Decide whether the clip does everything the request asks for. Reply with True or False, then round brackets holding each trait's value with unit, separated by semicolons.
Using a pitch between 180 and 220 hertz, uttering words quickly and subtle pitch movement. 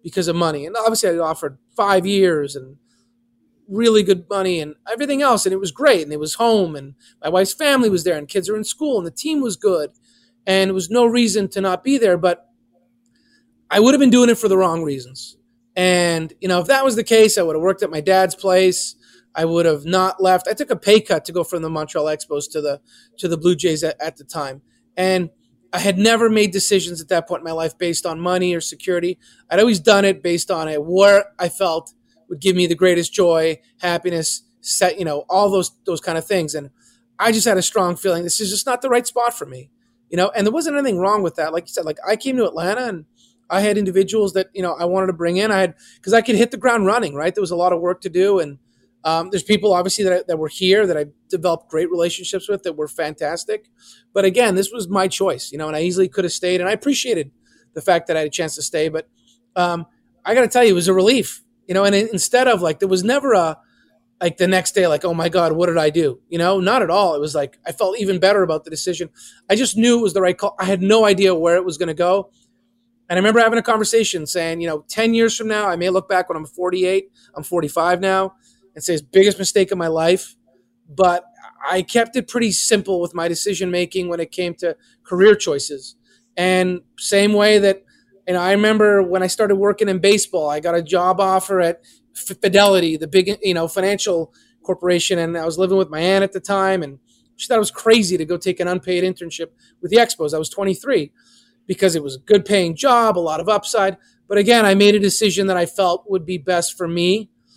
False (185 Hz; 250 wpm; 3.7 semitones)